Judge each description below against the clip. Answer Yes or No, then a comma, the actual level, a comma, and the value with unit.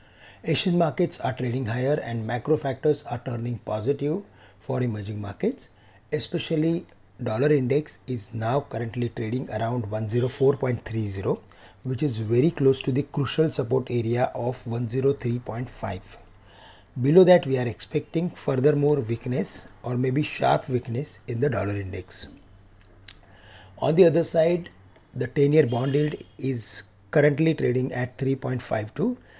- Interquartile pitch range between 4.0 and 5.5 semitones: Yes, average, 4.7 semitones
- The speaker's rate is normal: No, slow, 130 wpm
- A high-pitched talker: No, low, 125 Hz